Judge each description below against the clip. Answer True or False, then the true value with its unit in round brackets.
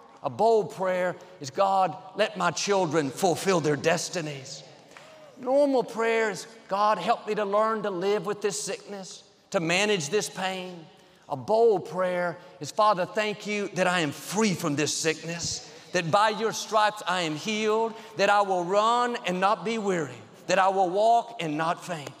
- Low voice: False (190 Hz)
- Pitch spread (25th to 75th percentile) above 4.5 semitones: False (3.5 semitones)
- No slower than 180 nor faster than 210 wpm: False (170 wpm)